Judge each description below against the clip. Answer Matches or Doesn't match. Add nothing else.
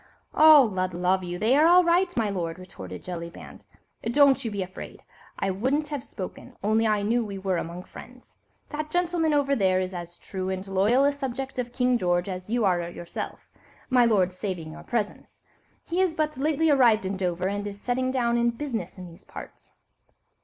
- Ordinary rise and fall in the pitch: Doesn't match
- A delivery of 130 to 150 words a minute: Doesn't match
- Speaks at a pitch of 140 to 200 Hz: Doesn't match